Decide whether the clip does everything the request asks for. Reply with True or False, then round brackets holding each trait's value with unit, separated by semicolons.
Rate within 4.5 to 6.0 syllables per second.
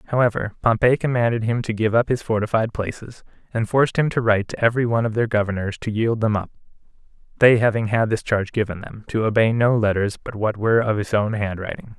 False (6.2 syllables/s)